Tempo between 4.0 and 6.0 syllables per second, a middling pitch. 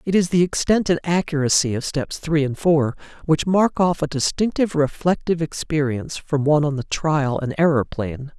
Yes: 5.3 syllables/s; medium, 155 Hz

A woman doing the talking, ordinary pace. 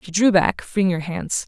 No: female; fast, 245 wpm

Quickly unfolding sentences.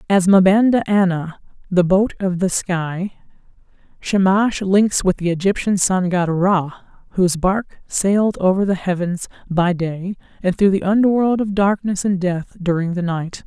No: average, 160 wpm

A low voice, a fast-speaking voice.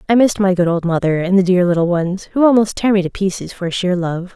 No: medium, 185 Hz; fast, 275 wpm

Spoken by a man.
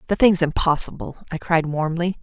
No: female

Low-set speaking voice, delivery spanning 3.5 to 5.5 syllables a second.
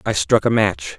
Yes: low, 105 Hz; 4.6 syllables/s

